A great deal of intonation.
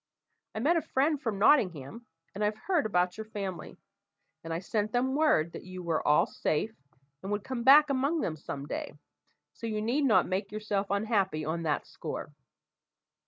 Yes: wide, 6.3 semitones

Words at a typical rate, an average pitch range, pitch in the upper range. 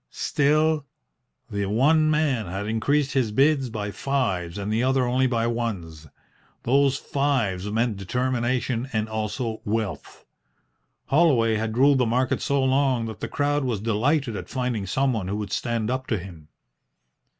No: average, 150 wpm; average, 4.1 semitones; low, 120 Hz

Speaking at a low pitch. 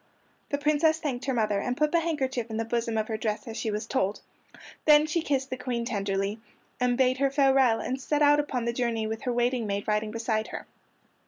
No: high, 245 Hz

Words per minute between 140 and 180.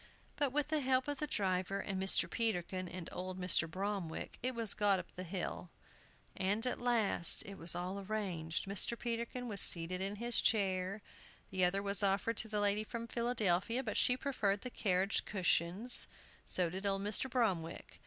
Yes: average, 175 wpm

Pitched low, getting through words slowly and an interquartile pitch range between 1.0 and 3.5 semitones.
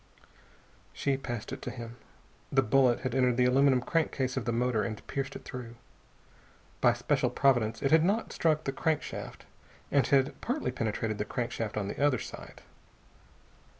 No: low, 130 Hz; average, 165 wpm; average, 3.0 semitones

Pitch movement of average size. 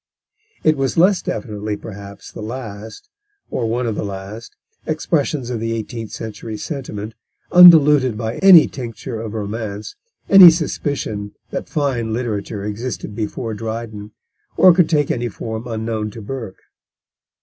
Yes: average, 4.2 semitones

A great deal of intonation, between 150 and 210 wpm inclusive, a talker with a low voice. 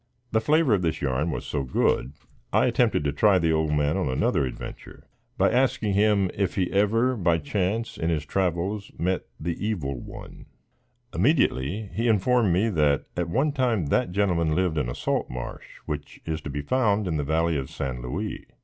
Yes: wide, 5.9 semitones; average, 190 wpm; very low, 90 Hz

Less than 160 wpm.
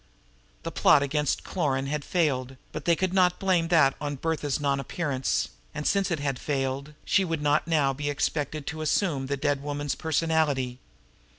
No: average, 175 wpm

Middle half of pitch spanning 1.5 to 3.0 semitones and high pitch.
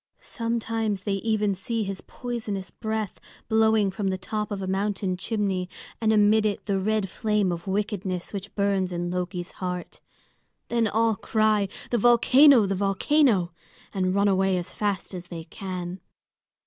Yes: average, 2.7 semitones; high, 200 Hz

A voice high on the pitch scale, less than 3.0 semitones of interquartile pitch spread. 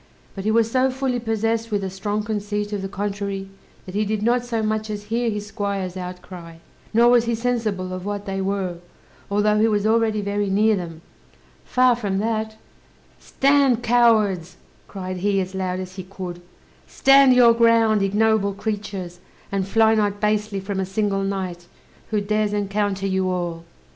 Yes: high, 205 Hz; narrow, 2.4 semitones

